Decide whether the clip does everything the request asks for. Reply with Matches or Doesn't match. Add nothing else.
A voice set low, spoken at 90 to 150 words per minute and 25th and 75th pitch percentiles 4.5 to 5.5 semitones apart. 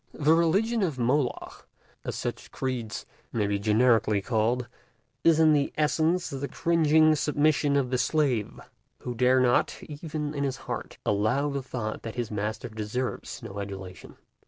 Matches